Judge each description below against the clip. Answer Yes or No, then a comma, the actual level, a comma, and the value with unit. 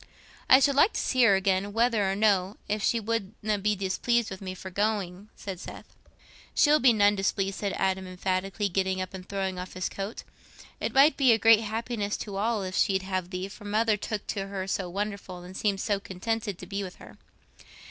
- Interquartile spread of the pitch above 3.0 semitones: No, narrow, 2.4 semitones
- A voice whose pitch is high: Yes, high, 200 Hz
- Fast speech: Yes, fast, 210 wpm